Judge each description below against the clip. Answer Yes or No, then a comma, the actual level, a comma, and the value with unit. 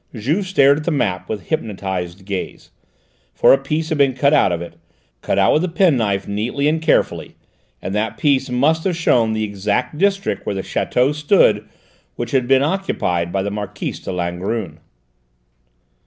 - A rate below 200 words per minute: Yes, average, 175 wpm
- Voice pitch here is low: Yes, low, 120 Hz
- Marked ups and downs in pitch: Yes, wide, 7.3 semitones